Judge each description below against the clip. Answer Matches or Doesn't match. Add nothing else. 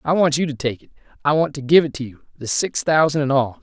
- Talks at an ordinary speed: Doesn't match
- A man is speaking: Matches